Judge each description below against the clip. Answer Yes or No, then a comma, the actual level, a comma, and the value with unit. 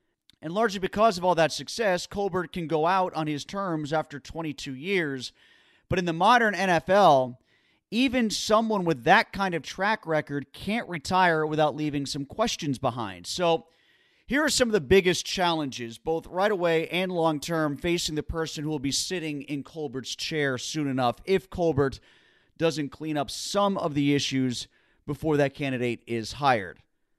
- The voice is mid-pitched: Yes, medium, 160 Hz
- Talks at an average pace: Yes, average, 170 wpm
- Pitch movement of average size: Yes, average, 4.7 semitones